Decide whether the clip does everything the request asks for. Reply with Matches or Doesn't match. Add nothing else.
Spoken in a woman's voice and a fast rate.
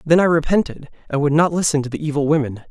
Doesn't match